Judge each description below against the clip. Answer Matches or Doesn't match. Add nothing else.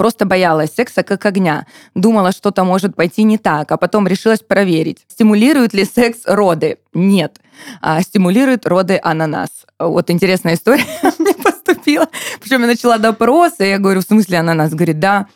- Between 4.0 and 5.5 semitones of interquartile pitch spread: Matches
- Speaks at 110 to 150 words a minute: Doesn't match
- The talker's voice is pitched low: Doesn't match